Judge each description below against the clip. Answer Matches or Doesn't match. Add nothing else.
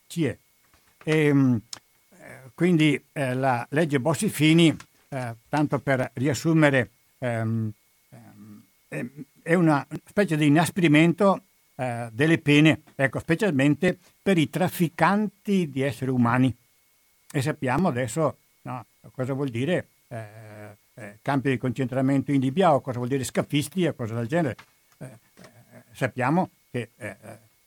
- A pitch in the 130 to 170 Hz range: Matches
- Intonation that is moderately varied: Matches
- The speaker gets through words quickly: Doesn't match